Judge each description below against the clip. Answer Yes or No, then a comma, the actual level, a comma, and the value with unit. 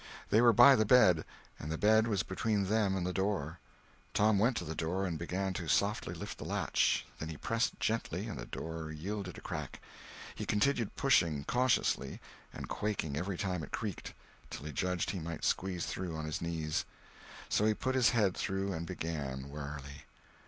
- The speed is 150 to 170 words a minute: No, average, 190 wpm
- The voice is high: No, very low, 95 Hz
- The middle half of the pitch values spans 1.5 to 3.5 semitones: No, average, 4.9 semitones